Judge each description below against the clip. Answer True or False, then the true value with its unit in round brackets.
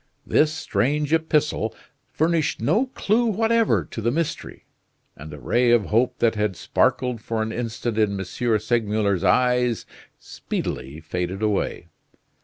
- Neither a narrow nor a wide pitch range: False (6.2 semitones)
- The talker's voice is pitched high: False (115 Hz)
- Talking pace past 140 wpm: False (135 wpm)